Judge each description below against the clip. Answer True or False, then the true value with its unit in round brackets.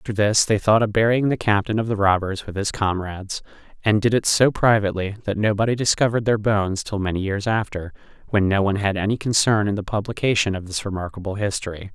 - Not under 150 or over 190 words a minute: False (205 wpm)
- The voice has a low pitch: True (105 Hz)